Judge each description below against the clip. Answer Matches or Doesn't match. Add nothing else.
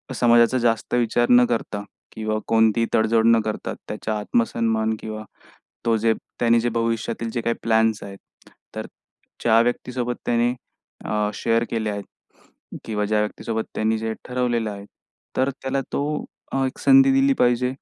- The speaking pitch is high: Doesn't match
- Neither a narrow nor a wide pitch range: Doesn't match